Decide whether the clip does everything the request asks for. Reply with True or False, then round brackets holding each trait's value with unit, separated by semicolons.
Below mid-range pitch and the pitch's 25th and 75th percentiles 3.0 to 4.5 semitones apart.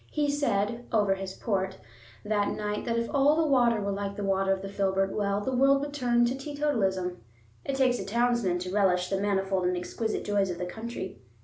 False (205 Hz; 4.0 semitones)